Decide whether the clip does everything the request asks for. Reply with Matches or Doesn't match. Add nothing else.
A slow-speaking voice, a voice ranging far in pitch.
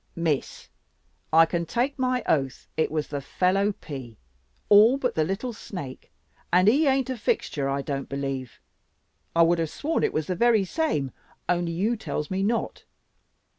Doesn't match